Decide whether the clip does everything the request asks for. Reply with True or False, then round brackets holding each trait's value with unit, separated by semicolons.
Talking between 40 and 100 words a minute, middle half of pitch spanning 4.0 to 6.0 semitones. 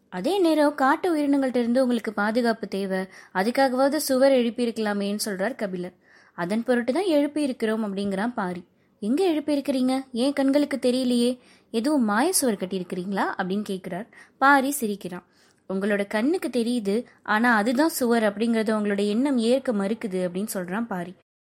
False (125 wpm; 5.0 semitones)